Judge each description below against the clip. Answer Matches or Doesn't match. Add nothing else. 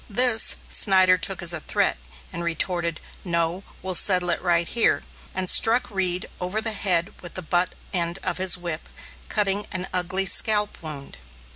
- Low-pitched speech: Doesn't match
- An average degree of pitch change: Doesn't match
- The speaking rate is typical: Matches